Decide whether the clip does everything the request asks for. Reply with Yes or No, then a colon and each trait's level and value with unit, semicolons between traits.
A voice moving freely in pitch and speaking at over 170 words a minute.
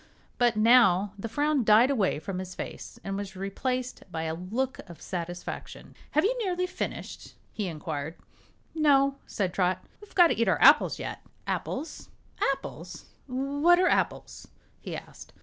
No: wide, 7.1 semitones; average, 155 wpm